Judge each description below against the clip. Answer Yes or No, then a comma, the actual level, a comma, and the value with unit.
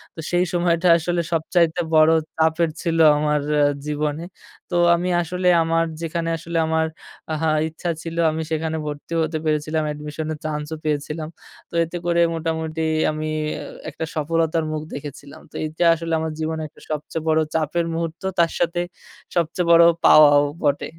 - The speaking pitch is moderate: Yes, medium, 160 Hz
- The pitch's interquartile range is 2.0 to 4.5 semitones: No, narrow, 1.4 semitones